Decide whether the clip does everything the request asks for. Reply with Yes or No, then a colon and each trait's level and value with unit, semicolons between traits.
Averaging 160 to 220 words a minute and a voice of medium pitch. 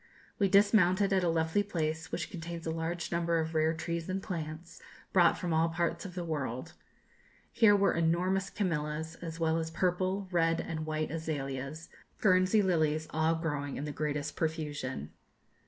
Yes: average, 165 wpm; medium, 165 Hz